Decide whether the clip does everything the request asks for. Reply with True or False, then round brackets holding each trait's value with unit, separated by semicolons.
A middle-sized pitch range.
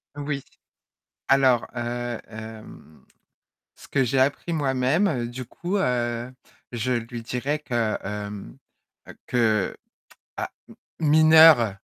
True (3.6 semitones)